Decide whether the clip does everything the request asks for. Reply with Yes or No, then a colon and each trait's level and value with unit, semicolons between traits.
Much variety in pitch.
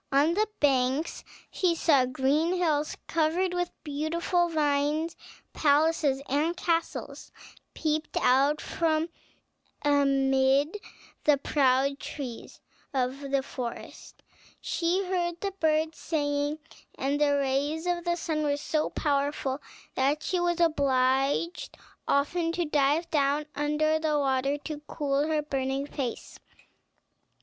No: average, 2.9 semitones